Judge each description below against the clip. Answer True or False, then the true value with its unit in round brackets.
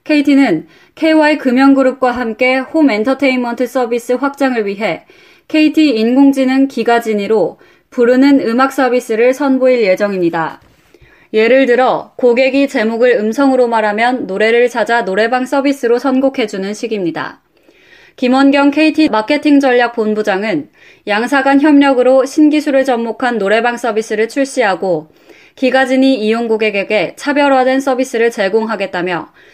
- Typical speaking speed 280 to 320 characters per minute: True (315 characters per minute)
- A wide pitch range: False (3.6 semitones)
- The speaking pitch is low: False (255 Hz)